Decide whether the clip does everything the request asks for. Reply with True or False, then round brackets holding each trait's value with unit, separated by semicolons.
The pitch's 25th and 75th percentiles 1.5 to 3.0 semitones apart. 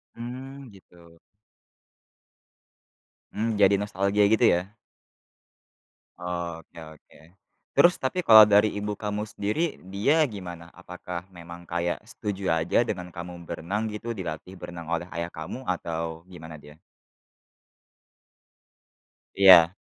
False (3.7 semitones)